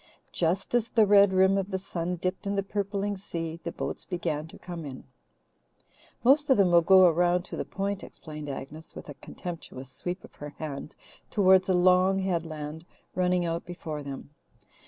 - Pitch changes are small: No, average, 3.2 semitones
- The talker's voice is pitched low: No, medium, 180 Hz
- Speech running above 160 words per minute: Yes, average, 180 wpm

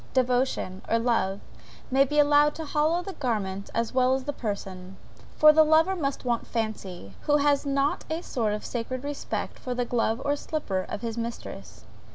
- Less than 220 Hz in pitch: No, very high, 255 Hz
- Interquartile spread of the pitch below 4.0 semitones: No, average, 4.7 semitones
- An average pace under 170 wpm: No, average, 185 wpm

